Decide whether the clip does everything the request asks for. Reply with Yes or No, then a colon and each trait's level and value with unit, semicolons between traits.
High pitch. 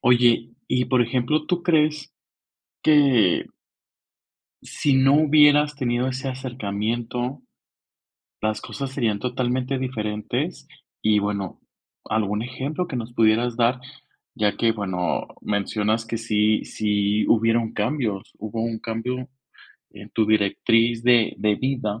No: low, 115 Hz